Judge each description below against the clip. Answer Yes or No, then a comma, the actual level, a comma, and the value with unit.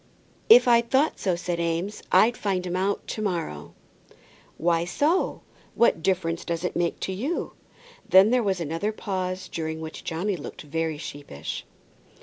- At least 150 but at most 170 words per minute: Yes, average, 155 wpm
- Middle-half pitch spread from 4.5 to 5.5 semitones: No, average, 3.9 semitones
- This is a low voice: No, medium, 180 Hz